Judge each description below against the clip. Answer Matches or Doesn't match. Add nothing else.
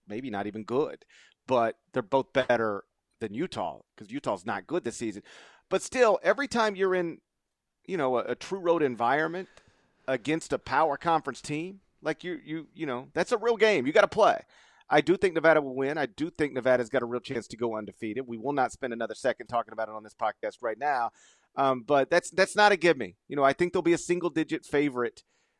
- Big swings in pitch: Matches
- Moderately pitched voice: Matches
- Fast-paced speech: Matches